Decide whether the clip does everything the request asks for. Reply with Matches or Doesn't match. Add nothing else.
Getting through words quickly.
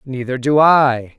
Doesn't match